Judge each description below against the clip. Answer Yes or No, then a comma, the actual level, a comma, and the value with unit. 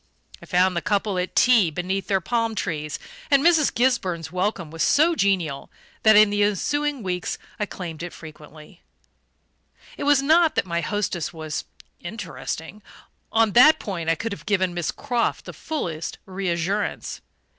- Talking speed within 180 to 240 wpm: No, average, 155 wpm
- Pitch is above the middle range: Yes, high, 195 Hz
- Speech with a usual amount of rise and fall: Yes, average, 5.0 semitones